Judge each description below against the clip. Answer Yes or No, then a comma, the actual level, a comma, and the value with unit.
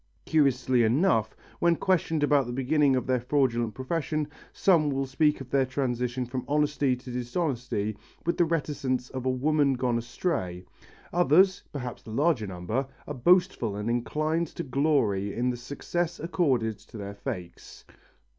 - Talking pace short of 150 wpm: No, average, 155 wpm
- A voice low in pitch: Yes, low, 130 Hz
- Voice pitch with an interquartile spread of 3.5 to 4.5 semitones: Yes, average, 4.2 semitones